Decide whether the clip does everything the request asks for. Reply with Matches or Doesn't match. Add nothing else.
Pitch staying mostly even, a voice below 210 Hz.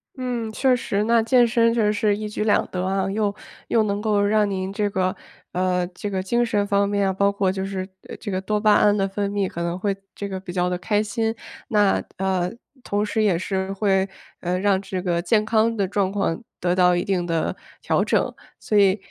Matches